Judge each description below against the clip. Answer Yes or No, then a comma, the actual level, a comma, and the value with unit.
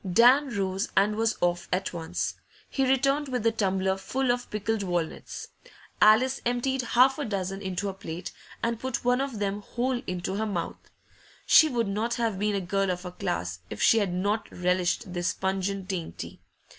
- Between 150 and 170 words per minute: No, average, 180 wpm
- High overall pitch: Yes, high, 205 Hz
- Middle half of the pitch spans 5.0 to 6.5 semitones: No, average, 4.5 semitones